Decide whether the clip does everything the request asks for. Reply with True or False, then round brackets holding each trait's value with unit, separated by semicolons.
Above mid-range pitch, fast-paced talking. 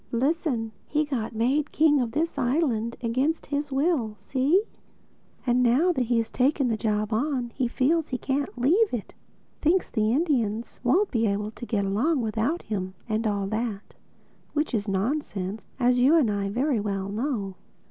False (245 Hz; 170 wpm)